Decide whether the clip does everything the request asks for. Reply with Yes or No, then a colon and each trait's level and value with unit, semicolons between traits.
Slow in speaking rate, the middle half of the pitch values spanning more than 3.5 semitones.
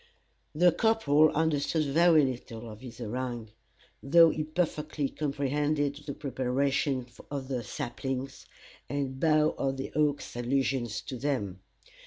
No: slow, 125 wpm; average, 2.8 semitones